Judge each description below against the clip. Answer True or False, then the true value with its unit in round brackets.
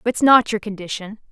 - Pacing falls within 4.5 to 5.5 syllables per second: True (5.3 syllables/s)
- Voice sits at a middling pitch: False (215 Hz)